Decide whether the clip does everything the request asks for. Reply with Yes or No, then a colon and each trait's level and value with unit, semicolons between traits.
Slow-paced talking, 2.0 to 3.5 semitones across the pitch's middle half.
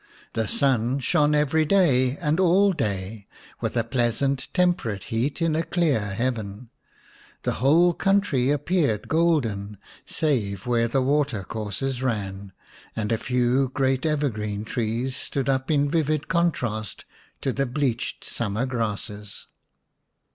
No: slow, 130 wpm; average, 5.2 semitones